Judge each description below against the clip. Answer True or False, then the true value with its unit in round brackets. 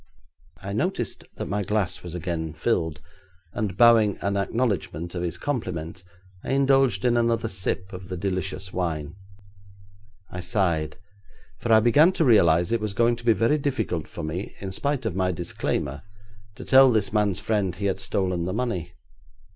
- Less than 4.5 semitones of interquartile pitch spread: False (4.9 semitones)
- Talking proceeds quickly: False (170 wpm)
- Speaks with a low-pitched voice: True (100 Hz)